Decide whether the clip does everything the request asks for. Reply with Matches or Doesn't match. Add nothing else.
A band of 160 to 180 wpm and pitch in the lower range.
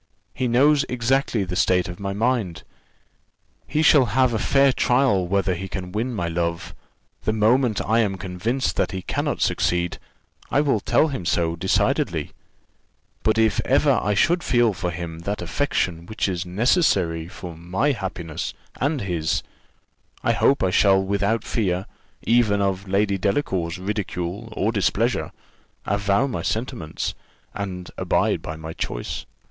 Doesn't match